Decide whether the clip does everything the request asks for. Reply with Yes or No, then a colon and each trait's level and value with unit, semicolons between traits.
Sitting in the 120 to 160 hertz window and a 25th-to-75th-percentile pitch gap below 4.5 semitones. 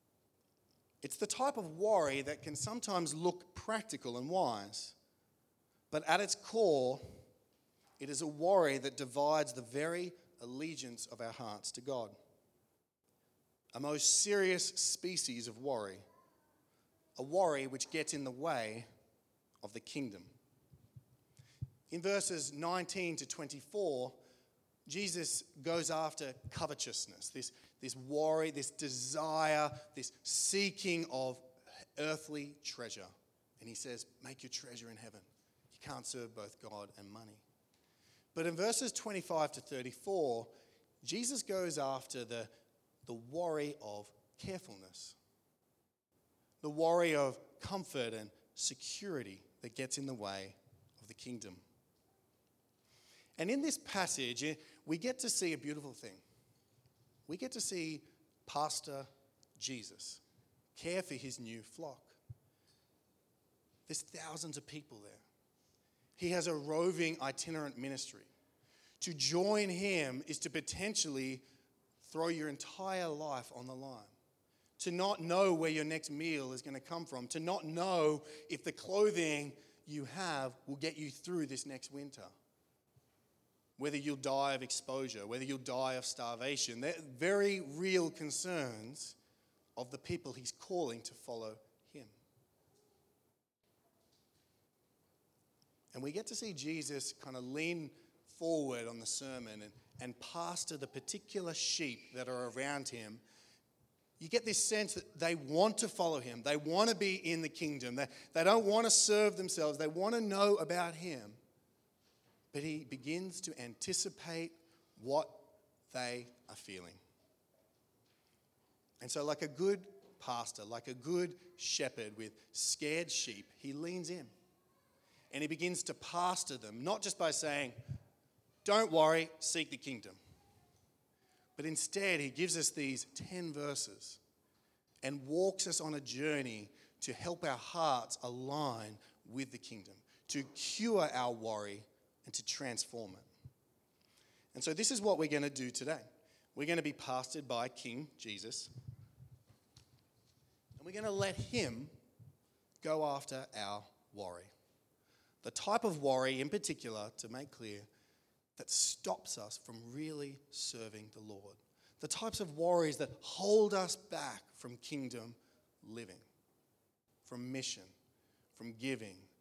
No: medium, 140 Hz; average, 5.3 semitones